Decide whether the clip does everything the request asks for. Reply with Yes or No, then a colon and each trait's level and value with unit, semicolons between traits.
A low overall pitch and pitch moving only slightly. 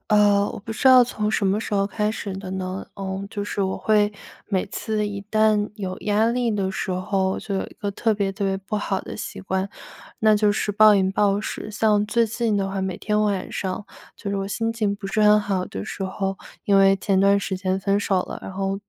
No: high, 200 Hz; narrow, 1.6 semitones